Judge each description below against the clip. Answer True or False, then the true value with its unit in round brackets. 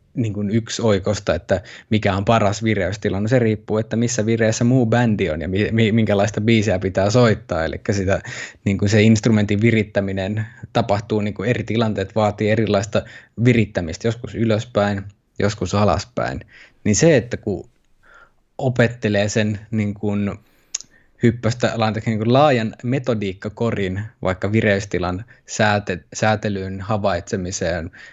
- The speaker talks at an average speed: True (125 wpm)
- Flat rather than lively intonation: True (2.2 semitones)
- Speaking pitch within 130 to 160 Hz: False (110 Hz)